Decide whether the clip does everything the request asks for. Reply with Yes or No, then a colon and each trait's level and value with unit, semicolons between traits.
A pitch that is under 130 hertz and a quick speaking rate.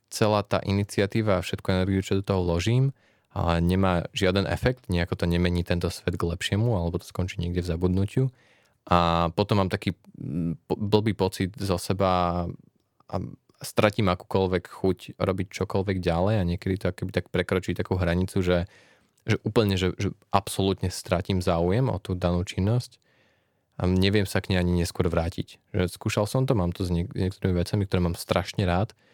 Yes: very low, 95 Hz; fast, 175 wpm